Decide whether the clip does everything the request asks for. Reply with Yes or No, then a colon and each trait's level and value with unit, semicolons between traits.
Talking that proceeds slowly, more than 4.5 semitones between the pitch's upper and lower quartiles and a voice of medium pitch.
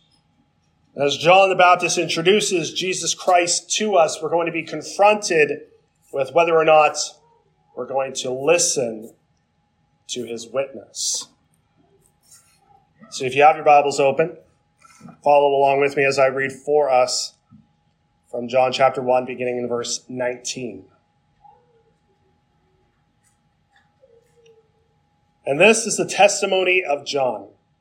Yes: slow, 120 wpm; wide, 5.5 semitones; medium, 155 Hz